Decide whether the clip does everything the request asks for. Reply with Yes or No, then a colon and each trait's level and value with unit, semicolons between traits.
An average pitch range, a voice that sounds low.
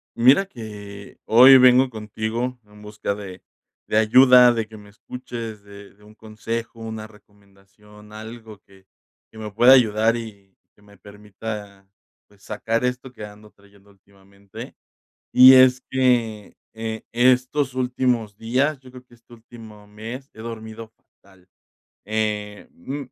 Yes: average, 3.0 semitones; low, 110 Hz